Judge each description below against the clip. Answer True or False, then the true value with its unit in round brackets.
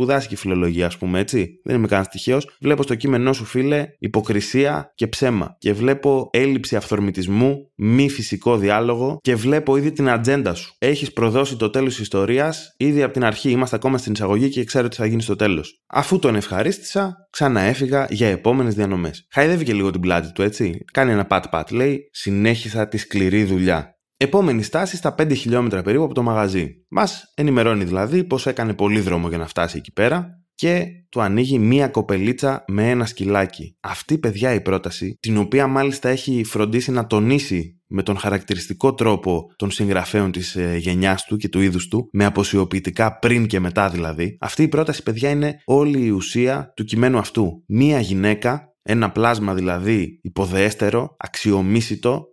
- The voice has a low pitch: True (115 Hz)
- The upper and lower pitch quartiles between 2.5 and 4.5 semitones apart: False (5.3 semitones)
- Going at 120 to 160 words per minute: False (170 wpm)